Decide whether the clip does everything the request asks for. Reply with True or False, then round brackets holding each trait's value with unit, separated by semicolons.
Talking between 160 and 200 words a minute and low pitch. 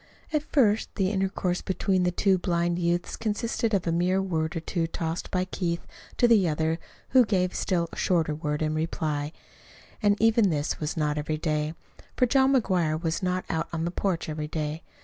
False (190 wpm; 175 Hz)